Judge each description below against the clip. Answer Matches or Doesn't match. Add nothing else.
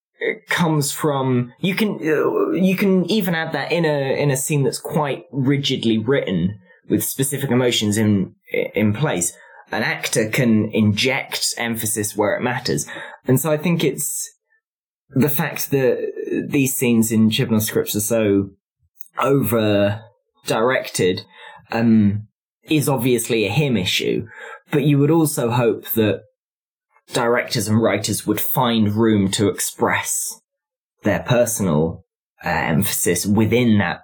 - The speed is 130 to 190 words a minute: Matches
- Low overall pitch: Matches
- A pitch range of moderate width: Doesn't match